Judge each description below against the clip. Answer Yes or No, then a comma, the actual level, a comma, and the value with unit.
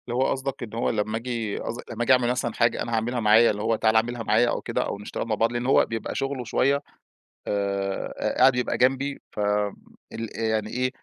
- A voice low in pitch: Yes, low, 115 Hz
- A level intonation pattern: Yes, narrow, 2.3 semitones